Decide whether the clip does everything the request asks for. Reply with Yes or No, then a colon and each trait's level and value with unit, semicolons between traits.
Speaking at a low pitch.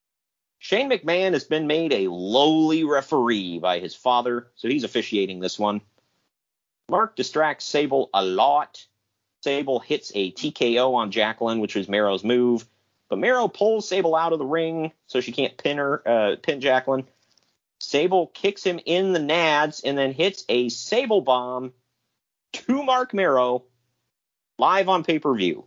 Yes: low, 130 Hz